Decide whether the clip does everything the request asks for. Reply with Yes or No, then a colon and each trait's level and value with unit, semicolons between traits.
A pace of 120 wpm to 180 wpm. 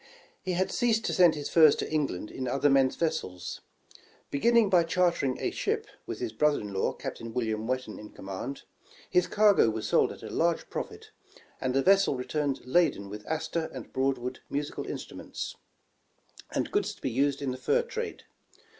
No: average, 190 wpm